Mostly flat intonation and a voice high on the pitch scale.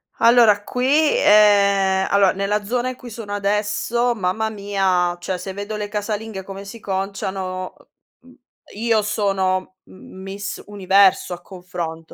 Yes: narrow, 2.1 semitones; high, 200 Hz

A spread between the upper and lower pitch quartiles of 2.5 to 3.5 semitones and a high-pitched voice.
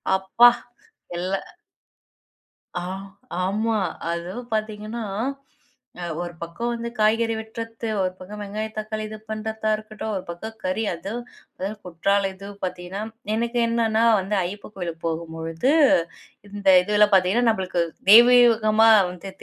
Yes: average, 3.2 semitones; high, 210 Hz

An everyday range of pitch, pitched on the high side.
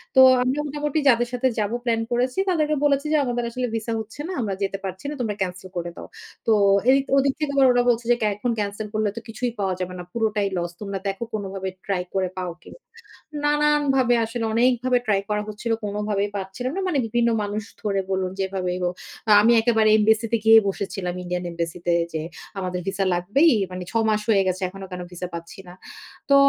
Yes: average, 4.3 semitones; high, 215 Hz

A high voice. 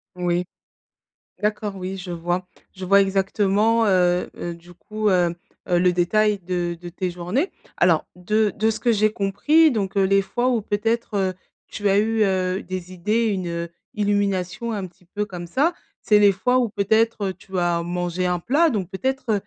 Yes: high, 195 Hz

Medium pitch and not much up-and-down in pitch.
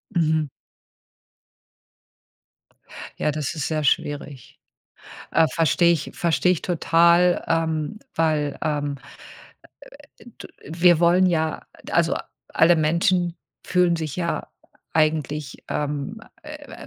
Yes: medium, 160 Hz; narrow, 2.2 semitones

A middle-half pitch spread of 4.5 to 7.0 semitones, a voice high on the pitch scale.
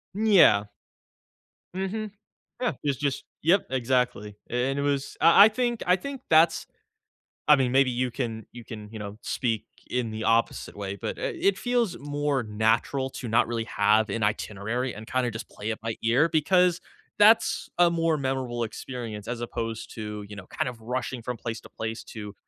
No: average, 5.2 semitones; low, 125 Hz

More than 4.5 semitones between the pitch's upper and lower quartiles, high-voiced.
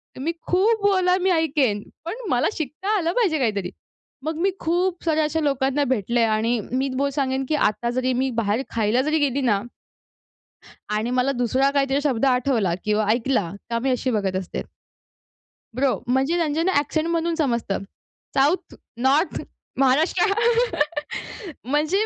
Yes: average, 5.1 semitones; very high, 270 Hz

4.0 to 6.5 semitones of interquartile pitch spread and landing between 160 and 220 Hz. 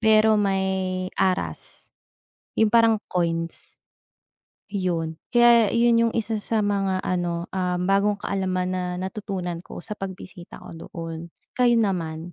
No: average, 3.1 semitones; high, 190 Hz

